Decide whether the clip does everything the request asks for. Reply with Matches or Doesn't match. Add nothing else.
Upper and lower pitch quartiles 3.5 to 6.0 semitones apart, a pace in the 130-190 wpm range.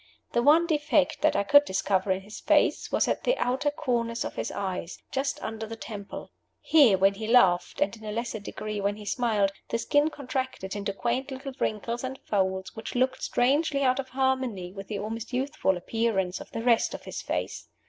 Doesn't match